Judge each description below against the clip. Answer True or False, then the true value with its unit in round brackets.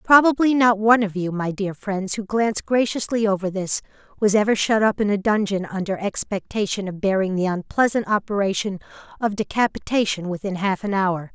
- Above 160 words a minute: True (175 wpm)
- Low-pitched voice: False (205 Hz)